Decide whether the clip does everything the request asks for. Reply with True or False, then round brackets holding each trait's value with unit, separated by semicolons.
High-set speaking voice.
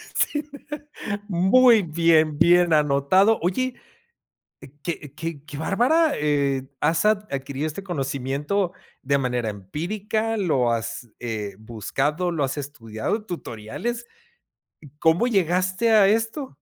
False (160 Hz)